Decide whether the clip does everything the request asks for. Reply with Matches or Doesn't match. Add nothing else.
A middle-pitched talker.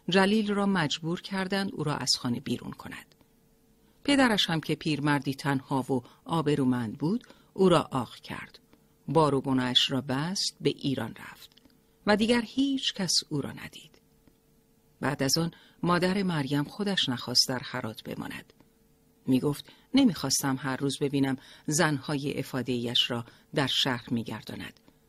Matches